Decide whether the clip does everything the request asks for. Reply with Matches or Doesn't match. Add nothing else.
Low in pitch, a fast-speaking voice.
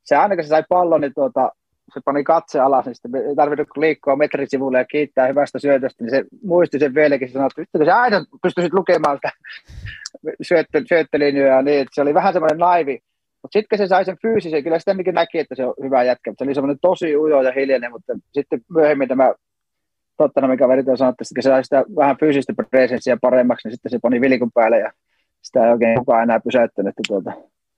Doesn't match